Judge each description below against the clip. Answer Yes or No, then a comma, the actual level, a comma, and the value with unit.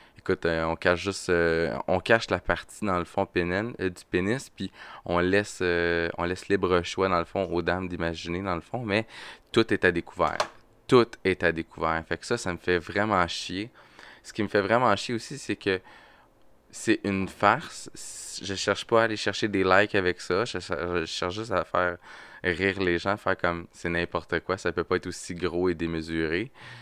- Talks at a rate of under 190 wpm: No, average, 215 wpm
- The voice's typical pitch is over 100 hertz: No, very low, 90 Hz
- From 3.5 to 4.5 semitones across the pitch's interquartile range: No, average, 2.8 semitones